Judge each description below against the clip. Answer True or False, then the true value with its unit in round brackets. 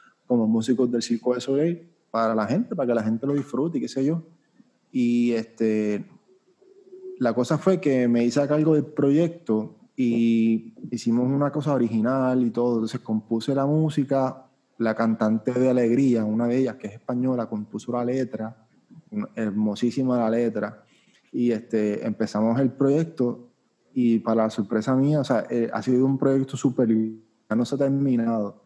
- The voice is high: False (125 Hz)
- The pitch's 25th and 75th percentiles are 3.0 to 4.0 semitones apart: True (3.5 semitones)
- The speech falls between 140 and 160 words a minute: False (170 wpm)